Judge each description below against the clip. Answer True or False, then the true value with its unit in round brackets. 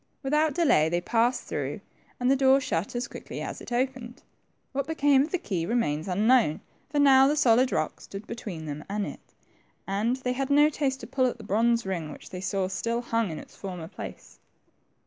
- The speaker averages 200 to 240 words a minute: True (205 wpm)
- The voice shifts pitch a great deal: True (5.7 semitones)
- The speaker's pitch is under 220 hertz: False (235 Hz)